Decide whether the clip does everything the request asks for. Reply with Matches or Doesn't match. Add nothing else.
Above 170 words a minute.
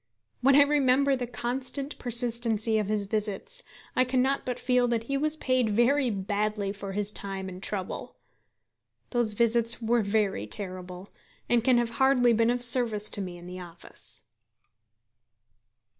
Doesn't match